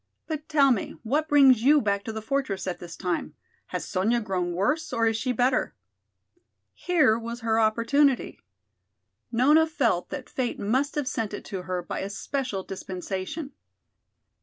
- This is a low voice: No, high, 230 Hz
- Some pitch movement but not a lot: No, wide, 5.9 semitones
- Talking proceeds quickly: No, average, 160 wpm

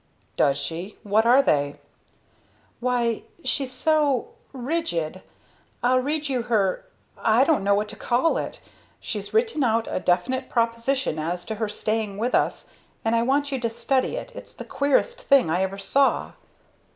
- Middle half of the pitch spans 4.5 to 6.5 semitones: Yes, average, 5.1 semitones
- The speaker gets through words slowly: No, average, 165 wpm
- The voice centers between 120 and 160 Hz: No, high, 235 Hz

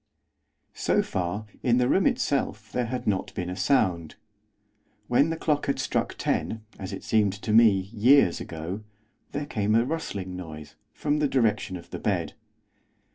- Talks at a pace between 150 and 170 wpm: Yes, average, 165 wpm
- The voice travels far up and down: Yes, wide, 5.8 semitones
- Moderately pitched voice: No, low, 110 Hz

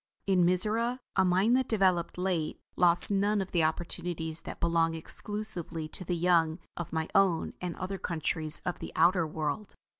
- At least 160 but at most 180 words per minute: Yes, average, 170 wpm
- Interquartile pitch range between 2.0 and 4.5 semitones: Yes, average, 3.0 semitones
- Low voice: No, medium, 175 Hz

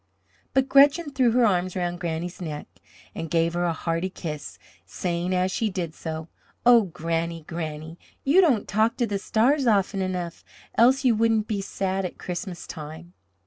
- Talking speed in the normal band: Yes, average, 170 wpm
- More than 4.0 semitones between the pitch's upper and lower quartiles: Yes, average, 5.2 semitones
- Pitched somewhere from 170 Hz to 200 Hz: Yes, medium, 185 Hz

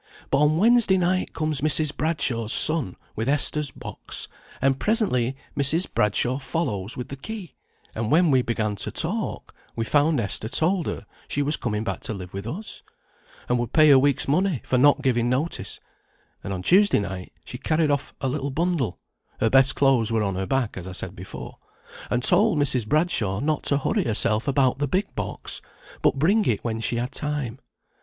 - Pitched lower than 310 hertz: Yes, low, 135 Hz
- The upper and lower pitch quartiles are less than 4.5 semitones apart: No, average, 5.3 semitones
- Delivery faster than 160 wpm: Yes, average, 190 wpm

